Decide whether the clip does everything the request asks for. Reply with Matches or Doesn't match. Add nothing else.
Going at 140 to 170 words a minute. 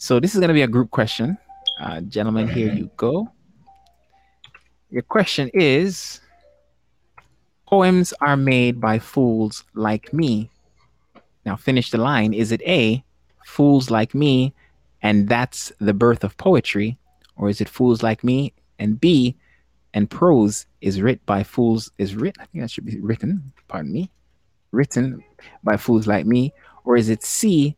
Matches